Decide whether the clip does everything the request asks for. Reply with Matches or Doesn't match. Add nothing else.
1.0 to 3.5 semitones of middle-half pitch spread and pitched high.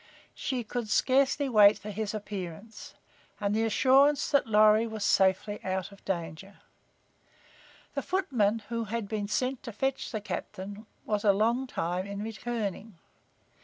Matches